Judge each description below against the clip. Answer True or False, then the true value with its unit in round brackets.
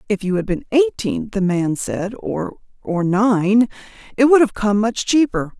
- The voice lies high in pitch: True (215 Hz)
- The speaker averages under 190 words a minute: True (170 wpm)